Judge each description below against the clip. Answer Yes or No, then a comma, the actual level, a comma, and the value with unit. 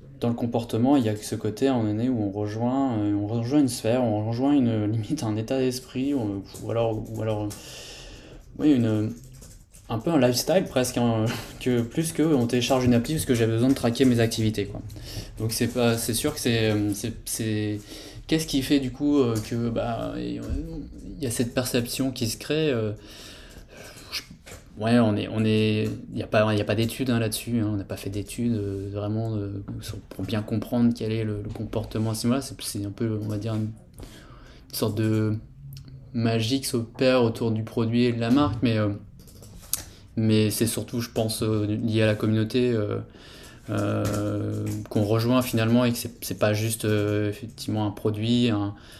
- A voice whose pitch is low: Yes, low, 115 Hz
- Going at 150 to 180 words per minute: No, average, 190 wpm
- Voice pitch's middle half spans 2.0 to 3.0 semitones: Yes, narrow, 2.5 semitones